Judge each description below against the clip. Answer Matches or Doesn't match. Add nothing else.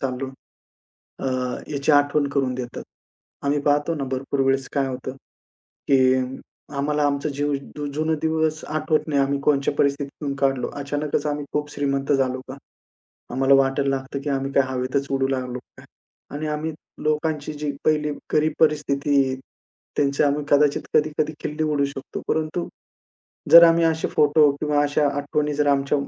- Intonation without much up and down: Matches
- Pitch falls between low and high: Matches